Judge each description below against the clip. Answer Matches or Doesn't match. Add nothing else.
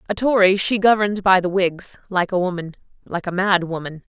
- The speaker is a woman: Matches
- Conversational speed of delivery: Matches